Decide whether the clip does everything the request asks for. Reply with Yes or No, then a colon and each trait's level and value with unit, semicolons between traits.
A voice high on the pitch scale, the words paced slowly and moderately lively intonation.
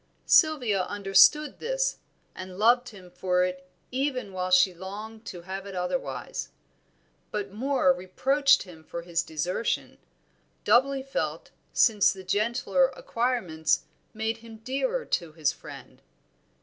No: high, 205 Hz; slow, 125 wpm; wide, 5.8 semitones